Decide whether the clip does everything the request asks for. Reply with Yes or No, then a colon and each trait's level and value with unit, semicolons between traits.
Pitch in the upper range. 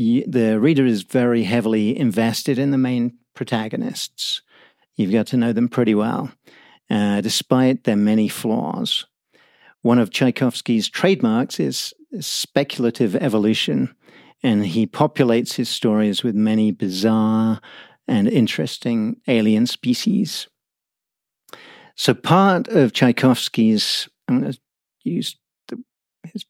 No: low, 120 Hz